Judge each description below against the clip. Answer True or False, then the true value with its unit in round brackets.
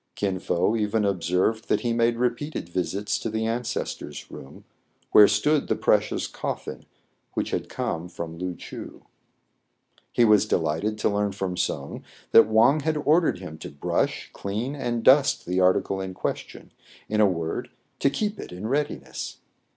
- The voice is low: True (105 Hz)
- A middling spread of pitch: True (4.6 semitones)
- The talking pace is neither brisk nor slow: True (160 wpm)